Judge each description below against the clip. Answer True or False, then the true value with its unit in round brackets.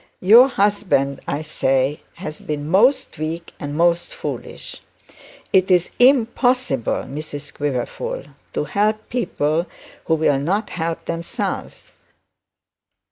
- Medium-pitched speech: True (170 Hz)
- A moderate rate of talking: False (110 wpm)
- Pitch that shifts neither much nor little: False (6.5 semitones)